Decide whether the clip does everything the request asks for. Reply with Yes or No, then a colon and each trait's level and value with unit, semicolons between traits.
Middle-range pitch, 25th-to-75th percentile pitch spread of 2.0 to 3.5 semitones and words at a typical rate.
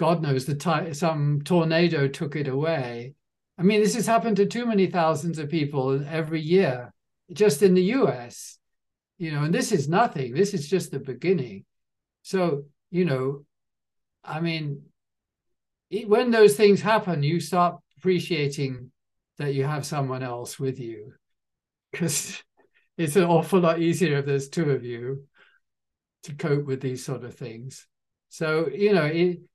No: medium, 160 Hz; average, 4.8 semitones; average, 160 wpm